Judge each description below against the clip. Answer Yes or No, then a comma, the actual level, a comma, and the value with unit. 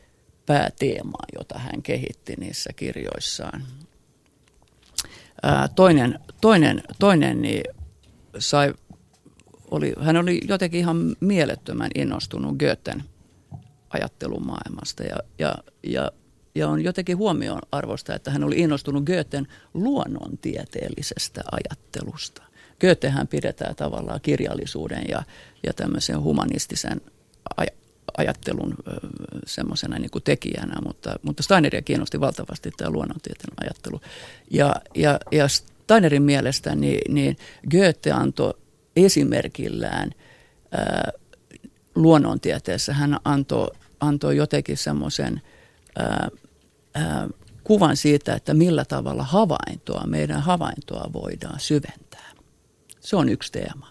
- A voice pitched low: No, medium, 145 Hz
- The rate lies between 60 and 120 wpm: Yes, average, 100 wpm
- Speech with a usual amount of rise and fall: Yes, average, 4.4 semitones